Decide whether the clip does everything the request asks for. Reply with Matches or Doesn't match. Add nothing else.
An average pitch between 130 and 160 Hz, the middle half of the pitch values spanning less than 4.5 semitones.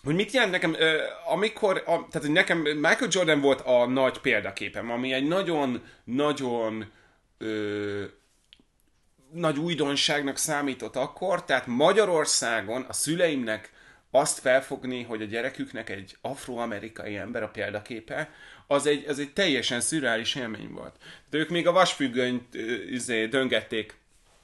Doesn't match